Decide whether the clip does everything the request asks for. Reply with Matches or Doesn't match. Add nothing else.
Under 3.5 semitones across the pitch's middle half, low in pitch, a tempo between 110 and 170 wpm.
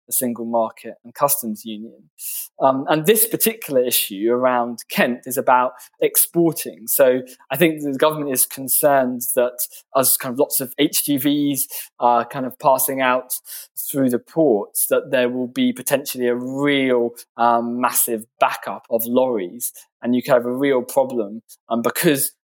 Matches